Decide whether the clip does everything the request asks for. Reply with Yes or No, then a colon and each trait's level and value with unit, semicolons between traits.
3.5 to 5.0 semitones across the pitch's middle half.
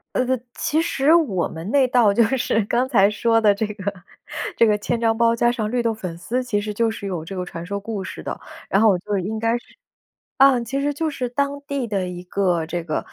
Yes: average, 4.1 semitones